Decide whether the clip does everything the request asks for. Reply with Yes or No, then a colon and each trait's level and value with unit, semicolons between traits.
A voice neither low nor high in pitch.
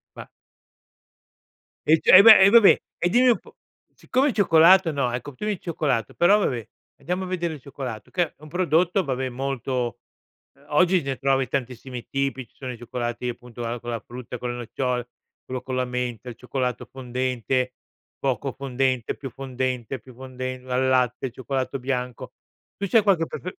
No: low, 130 Hz